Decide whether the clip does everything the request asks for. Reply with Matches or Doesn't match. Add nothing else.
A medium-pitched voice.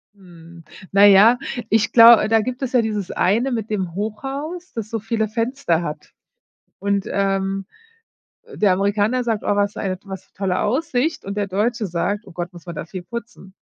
Doesn't match